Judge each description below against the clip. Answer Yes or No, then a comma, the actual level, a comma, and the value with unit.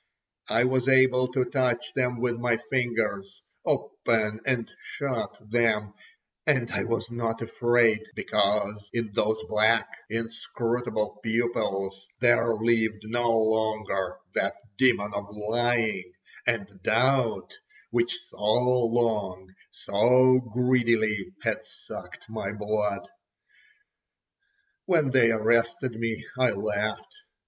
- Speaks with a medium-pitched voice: No, low, 115 Hz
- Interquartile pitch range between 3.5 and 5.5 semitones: No, narrow, 2.5 semitones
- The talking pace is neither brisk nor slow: No, slow, 105 wpm